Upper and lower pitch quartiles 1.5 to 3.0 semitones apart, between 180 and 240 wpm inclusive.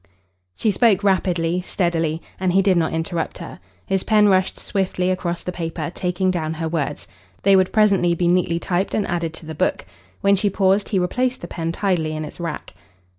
Yes: narrow, 2.6 semitones; average, 195 wpm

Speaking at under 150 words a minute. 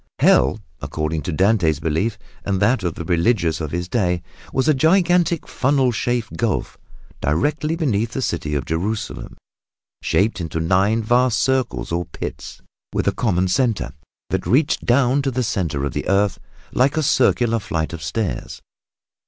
No: average, 160 wpm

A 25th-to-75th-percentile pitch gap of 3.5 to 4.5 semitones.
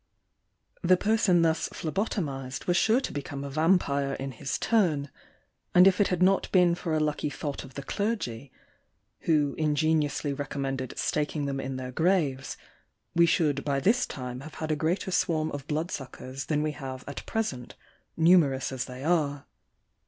Yes: average, 4.2 semitones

